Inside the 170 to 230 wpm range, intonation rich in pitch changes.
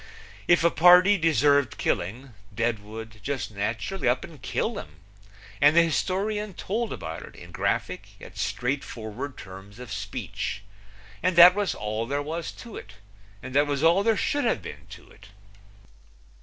No: average, 155 wpm; wide, 8.2 semitones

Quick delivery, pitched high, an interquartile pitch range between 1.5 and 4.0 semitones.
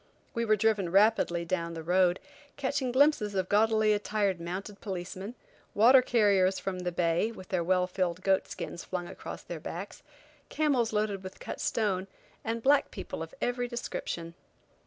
No: average, 160 wpm; high, 200 Hz; average, 3.7 semitones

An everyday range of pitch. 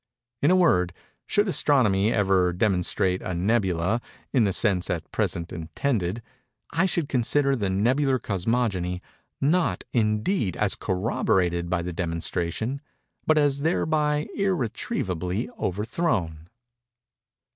No: wide, 7.6 semitones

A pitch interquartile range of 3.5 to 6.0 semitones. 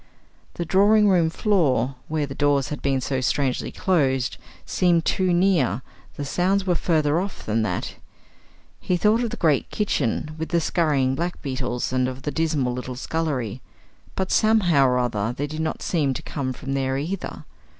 Yes: average, 5.1 semitones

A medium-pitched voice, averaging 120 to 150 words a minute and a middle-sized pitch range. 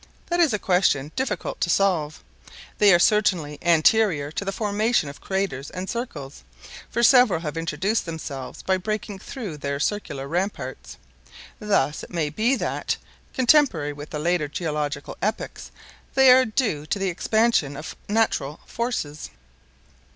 No: medium, 180 Hz; average, 145 wpm; wide, 6.5 semitones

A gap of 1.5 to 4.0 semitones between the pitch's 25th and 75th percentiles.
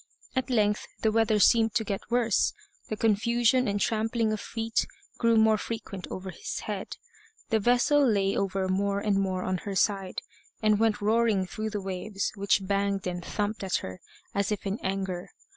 Yes: narrow, 2.4 semitones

